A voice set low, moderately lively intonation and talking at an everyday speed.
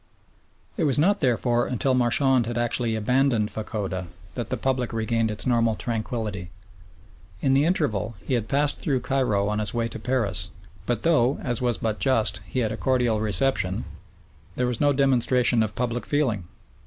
Yes: low, 120 Hz; average, 3.2 semitones; average, 170 wpm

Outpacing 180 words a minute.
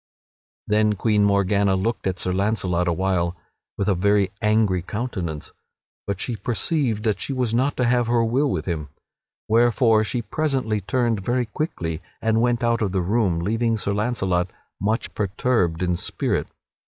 No: average, 160 wpm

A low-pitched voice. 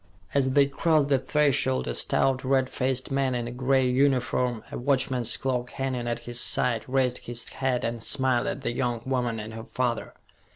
Yes: low, 130 Hz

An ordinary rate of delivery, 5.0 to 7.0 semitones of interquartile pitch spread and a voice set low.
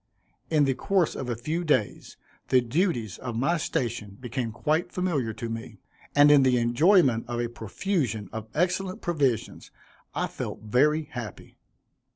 Yes: average, 155 wpm; wide, 5.5 semitones; low, 130 Hz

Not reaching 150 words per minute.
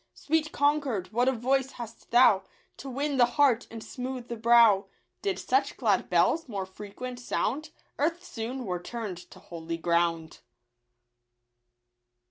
Yes: average, 140 wpm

